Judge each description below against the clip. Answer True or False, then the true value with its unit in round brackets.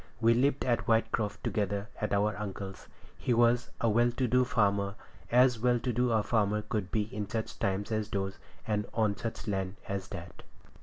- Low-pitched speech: True (110 Hz)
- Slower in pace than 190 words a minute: False (195 wpm)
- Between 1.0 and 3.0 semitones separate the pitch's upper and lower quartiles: True (2.7 semitones)